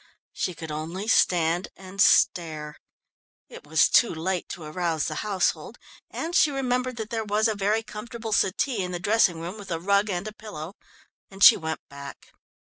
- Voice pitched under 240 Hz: Yes, high, 190 Hz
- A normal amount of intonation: Yes, average, 4.7 semitones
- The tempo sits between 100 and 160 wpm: No, average, 180 wpm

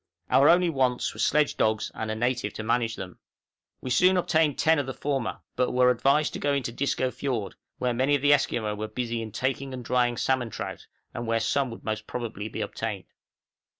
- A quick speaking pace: Yes, fast, 210 wpm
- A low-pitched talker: Yes, low, 125 Hz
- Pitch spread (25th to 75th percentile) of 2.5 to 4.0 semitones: Yes, average, 3.4 semitones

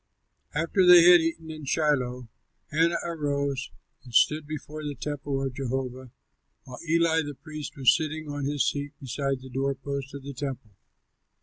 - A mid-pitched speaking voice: Yes, medium, 145 Hz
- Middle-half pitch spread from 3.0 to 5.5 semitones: No, narrow, 2.6 semitones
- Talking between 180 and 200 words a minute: No, average, 165 wpm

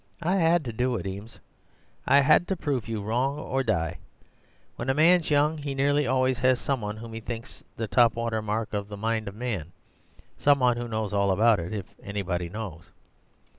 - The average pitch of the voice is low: Yes, low, 115 Hz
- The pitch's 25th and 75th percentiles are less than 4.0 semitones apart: No, average, 4.4 semitones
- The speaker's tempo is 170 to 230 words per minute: Yes, fast, 205 wpm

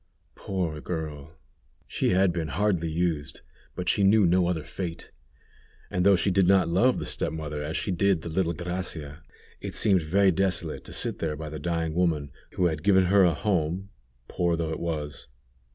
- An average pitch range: Yes, average, 3.1 semitones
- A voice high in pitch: No, very low, 85 Hz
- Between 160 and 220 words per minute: Yes, average, 185 wpm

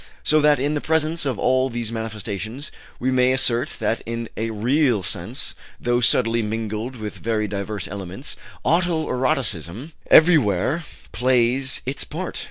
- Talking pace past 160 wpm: No, average, 145 wpm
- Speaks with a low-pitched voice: Yes, low, 120 Hz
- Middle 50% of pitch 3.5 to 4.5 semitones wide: Yes, average, 4.0 semitones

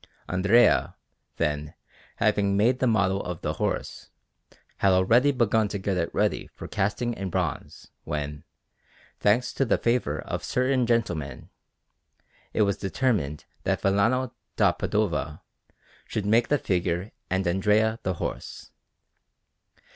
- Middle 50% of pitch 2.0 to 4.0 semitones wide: No, average, 4.5 semitones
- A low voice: Yes, low, 100 Hz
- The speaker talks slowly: Yes, slow, 130 wpm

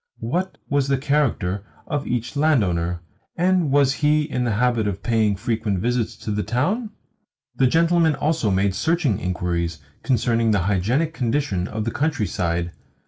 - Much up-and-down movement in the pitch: Yes, wide, 6.6 semitones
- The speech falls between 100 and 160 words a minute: Yes, average, 150 wpm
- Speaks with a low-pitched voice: Yes, low, 120 Hz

